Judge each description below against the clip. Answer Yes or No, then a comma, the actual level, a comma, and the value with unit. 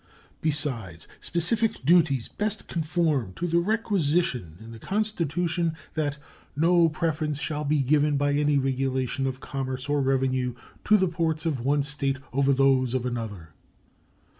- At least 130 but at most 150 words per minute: Yes, average, 140 wpm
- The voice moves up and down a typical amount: Yes, average, 4.1 semitones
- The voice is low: No, medium, 145 Hz